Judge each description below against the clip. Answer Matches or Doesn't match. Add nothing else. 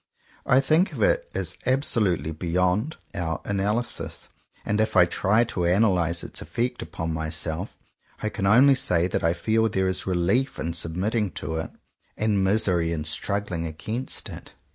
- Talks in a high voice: Doesn't match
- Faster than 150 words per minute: Matches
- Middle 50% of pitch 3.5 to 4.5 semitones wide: Doesn't match